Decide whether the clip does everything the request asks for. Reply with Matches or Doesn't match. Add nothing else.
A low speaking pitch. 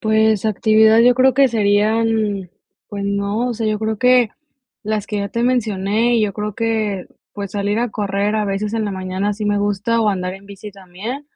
Doesn't match